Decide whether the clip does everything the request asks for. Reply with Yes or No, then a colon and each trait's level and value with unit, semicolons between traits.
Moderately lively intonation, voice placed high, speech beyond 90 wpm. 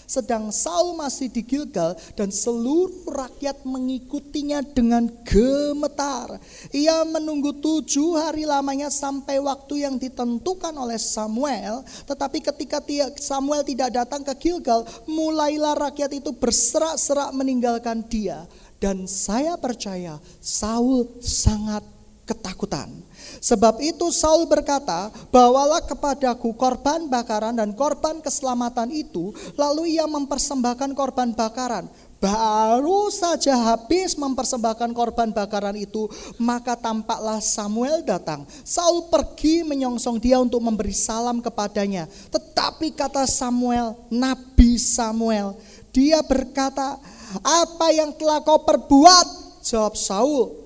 Yes: average, 4.4 semitones; very high, 260 Hz; average, 110 wpm